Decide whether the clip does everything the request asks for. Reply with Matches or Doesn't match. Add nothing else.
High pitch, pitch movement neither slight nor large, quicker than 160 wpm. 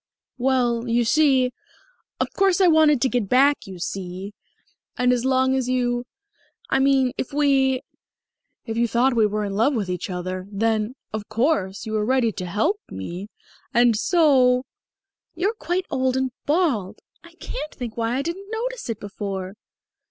Matches